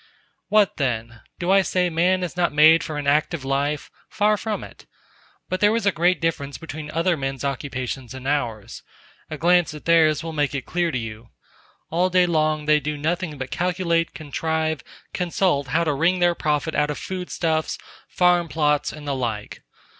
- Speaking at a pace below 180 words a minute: No, average, 185 wpm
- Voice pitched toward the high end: No, medium, 155 Hz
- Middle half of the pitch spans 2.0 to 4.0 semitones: Yes, average, 3.7 semitones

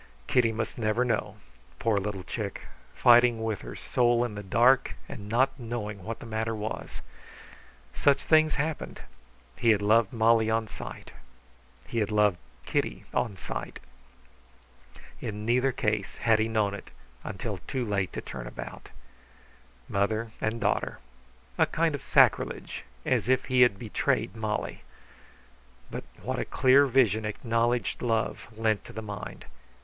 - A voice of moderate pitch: No, low, 115 Hz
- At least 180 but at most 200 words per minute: No, average, 145 wpm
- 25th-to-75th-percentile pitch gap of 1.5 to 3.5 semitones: Yes, narrow, 2.4 semitones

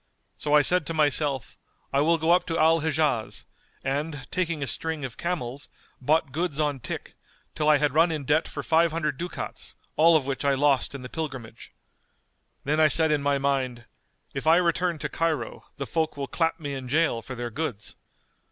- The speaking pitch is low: No, medium, 150 Hz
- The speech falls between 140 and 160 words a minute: No, average, 190 wpm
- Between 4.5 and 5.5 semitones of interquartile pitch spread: No, average, 2.9 semitones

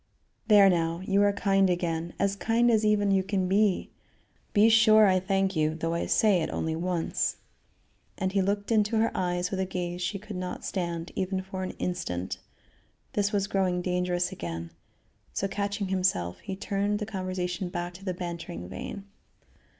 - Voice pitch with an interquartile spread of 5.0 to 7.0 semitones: No, narrow, 2.4 semitones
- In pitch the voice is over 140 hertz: Yes, high, 190 Hz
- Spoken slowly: No, average, 175 wpm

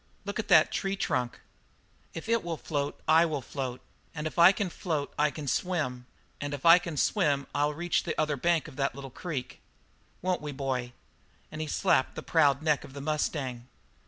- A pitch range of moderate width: Yes, average, 3.5 semitones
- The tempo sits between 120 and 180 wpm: No, average, 195 wpm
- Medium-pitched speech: Yes, medium, 150 Hz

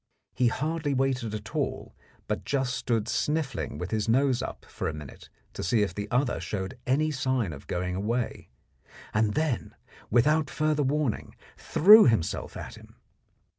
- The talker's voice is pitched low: Yes, low, 125 Hz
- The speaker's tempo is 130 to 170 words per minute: Yes, average, 160 wpm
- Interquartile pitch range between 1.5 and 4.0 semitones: No, average, 5.3 semitones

